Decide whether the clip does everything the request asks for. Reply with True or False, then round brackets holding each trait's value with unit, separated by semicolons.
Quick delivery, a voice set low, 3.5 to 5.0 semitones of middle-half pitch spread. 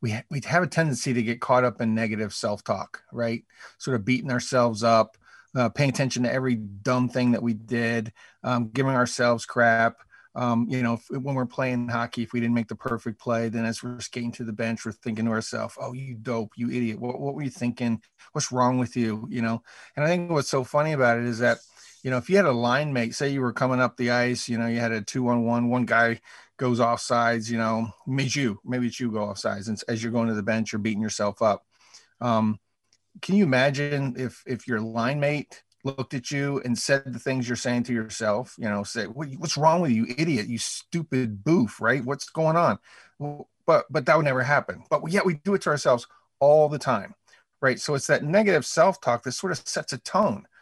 False (235 wpm; 120 Hz; 2.4 semitones)